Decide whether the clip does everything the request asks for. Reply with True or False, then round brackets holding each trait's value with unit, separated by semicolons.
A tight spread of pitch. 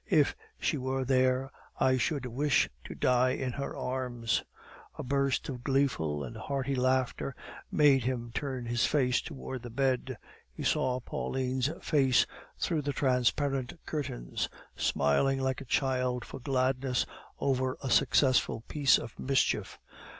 True (1.4 semitones)